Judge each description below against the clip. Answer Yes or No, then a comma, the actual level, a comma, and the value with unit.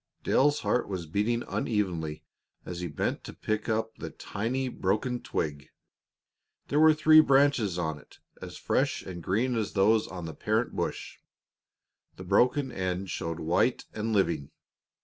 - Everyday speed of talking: Yes, average, 150 wpm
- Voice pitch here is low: Yes, low, 105 Hz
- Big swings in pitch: Yes, wide, 6.0 semitones